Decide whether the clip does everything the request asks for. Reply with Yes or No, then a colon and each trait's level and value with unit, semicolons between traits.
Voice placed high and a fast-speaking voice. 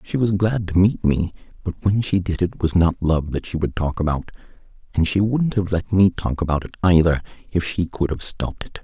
No: very low, 90 Hz; fast, 240 wpm